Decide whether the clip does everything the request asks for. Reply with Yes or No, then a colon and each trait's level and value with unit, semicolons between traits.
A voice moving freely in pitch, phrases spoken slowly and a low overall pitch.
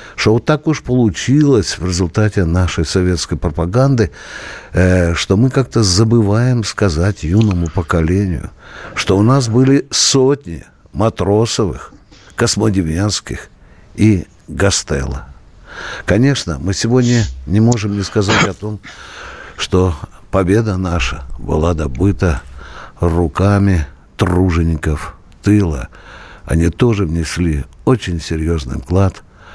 No: average, 4.4 semitones; slow, 100 wpm; very low, 95 Hz